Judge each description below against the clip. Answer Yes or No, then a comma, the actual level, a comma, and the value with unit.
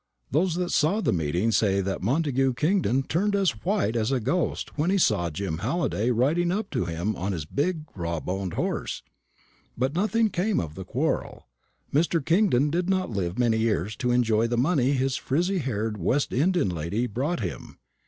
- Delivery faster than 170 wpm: Yes, average, 185 wpm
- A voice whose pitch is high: No, low, 125 Hz